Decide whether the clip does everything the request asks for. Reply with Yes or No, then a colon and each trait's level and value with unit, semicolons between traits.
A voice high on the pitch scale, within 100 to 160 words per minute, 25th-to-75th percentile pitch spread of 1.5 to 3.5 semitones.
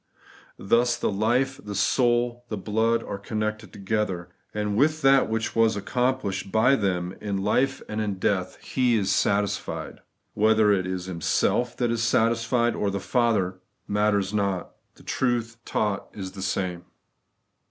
No: low, 105 Hz; average, 155 wpm; average, 3.2 semitones